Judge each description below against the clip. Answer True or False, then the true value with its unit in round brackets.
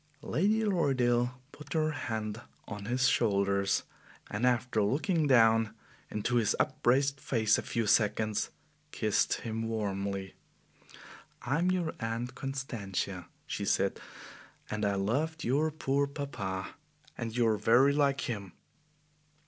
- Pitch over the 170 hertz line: False (120 Hz)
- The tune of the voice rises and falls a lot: False (4.7 semitones)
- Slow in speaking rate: True (125 wpm)